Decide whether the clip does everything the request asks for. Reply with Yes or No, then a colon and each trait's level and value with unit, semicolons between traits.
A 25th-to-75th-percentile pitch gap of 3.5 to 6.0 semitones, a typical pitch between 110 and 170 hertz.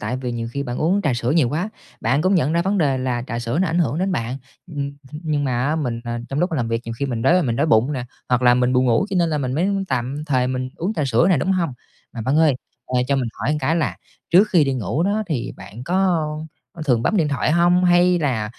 Yes: wide, 5.4 semitones; medium, 140 Hz